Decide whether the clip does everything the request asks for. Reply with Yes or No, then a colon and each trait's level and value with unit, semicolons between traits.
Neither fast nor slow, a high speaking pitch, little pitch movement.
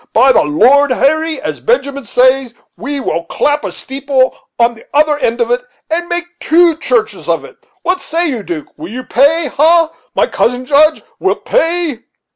No: average, 180 wpm; very high, 280 Hz; average, 4.8 semitones